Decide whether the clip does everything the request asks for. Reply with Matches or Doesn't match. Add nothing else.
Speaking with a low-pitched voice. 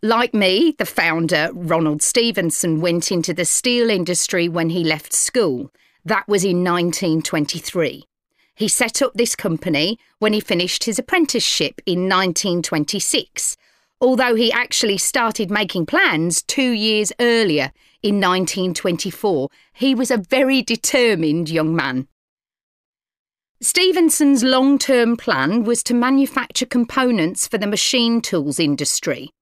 Doesn't match